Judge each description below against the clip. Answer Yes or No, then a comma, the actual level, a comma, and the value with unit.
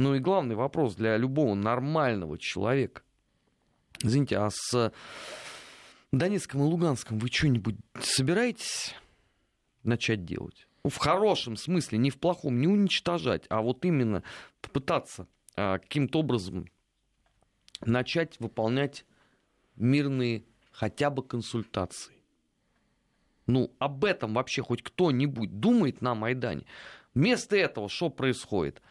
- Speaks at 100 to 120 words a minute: Yes, slow, 110 wpm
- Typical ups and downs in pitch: Yes, average, 4.3 semitones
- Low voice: Yes, low, 125 Hz